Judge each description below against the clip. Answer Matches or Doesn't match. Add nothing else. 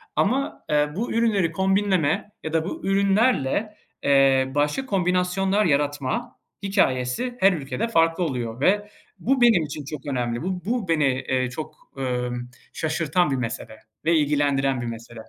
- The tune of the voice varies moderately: Doesn't match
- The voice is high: Doesn't match